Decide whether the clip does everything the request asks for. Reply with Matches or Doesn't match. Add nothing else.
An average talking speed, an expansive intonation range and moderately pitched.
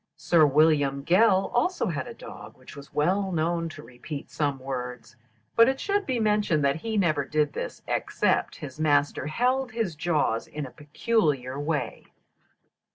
Matches